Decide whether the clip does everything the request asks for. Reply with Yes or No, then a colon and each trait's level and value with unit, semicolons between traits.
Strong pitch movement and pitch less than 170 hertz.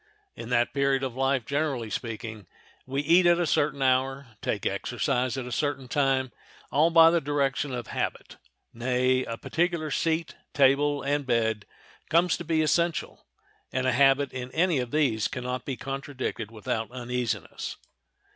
No: average, 2.9 semitones; low, 135 Hz